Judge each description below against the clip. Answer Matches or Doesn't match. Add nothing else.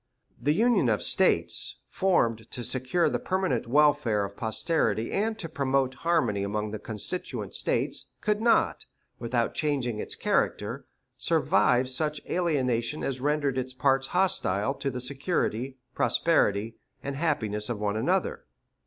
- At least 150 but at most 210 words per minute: Doesn't match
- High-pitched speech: Doesn't match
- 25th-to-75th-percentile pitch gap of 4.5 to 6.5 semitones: Matches